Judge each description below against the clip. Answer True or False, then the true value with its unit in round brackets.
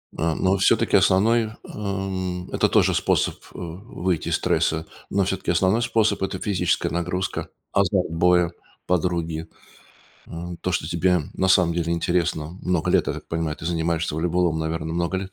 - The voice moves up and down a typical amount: False (2.3 semitones)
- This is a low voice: True (90 Hz)